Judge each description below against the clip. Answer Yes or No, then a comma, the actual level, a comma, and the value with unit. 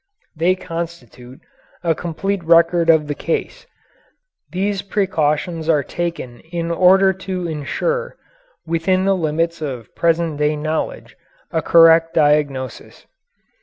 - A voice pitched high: No, medium, 165 Hz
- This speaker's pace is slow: Yes, slow, 115 wpm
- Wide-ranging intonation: No, average, 3.1 semitones